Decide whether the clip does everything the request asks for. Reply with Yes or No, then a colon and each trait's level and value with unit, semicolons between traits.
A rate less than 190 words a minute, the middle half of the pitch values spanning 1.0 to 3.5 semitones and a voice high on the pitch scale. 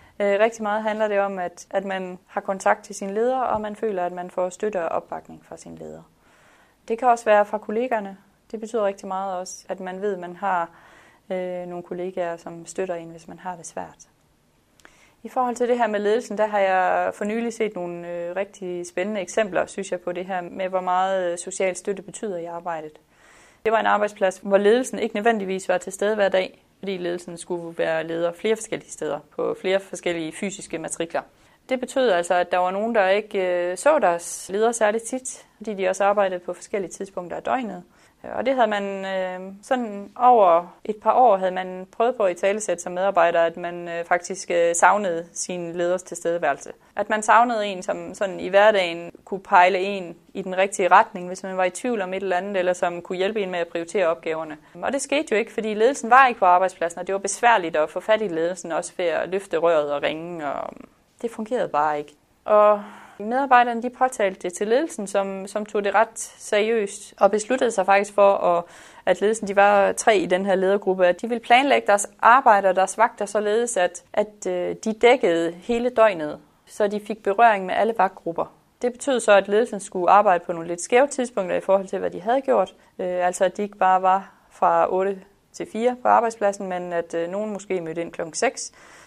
No: average, 210 wpm; average, 3.2 semitones; high, 195 Hz